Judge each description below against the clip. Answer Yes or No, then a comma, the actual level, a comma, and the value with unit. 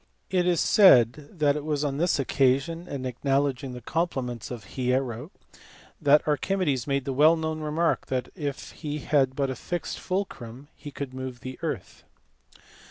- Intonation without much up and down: No, average, 3.4 semitones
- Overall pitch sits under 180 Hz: Yes, medium, 140 Hz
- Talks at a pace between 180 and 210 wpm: No, average, 160 wpm